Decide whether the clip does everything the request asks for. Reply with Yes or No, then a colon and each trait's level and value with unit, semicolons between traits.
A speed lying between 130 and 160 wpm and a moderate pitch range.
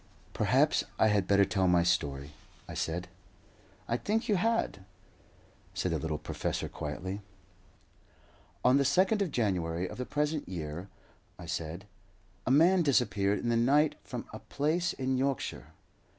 No: average, 150 wpm; wide, 8.7 semitones